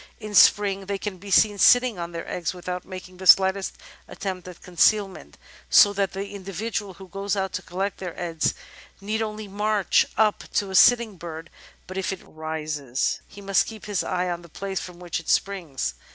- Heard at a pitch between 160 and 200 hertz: Yes, high, 190 Hz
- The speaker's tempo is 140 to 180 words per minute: No, average, 195 wpm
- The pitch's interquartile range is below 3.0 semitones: Yes, narrow, 2.4 semitones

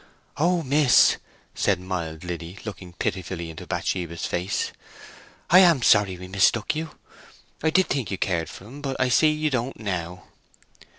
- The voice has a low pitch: Yes, low, 100 Hz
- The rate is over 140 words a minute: Yes, average, 165 wpm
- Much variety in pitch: Yes, wide, 8.0 semitones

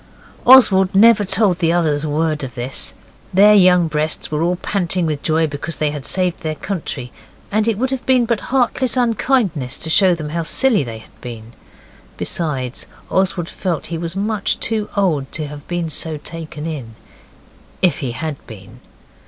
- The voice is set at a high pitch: No, medium, 165 Hz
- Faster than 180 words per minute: No, average, 175 wpm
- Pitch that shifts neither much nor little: Yes, average, 5.0 semitones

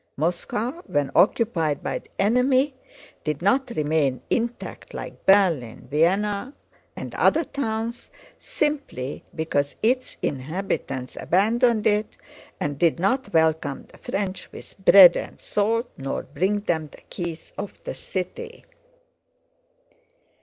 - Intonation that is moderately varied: No, wide, 6.9 semitones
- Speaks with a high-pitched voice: Yes, high, 195 Hz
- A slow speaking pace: Yes, slow, 120 wpm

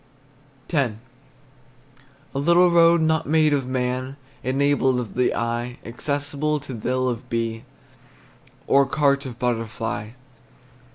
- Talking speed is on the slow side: Yes, slow, 115 wpm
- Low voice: Yes, low, 130 Hz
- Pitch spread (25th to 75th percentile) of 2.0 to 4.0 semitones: Yes, average, 3.0 semitones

